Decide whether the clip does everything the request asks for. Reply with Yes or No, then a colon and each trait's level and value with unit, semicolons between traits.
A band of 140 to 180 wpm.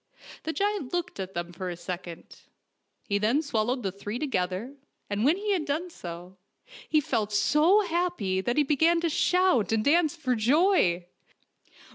Yes: average, 165 wpm